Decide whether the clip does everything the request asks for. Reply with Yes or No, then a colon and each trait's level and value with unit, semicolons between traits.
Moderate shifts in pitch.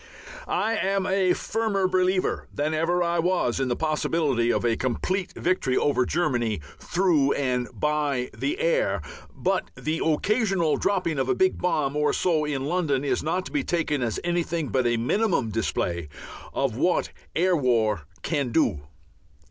No: wide, 6.1 semitones